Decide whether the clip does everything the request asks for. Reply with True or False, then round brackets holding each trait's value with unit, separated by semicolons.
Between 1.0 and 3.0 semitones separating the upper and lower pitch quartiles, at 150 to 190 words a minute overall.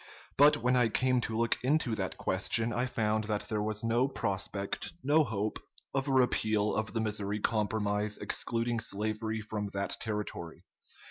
True (2.4 semitones; 160 wpm)